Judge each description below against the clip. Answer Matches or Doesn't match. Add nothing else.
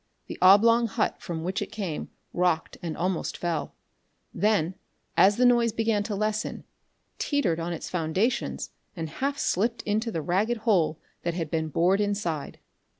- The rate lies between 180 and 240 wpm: Doesn't match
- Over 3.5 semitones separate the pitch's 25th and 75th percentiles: Matches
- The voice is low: Doesn't match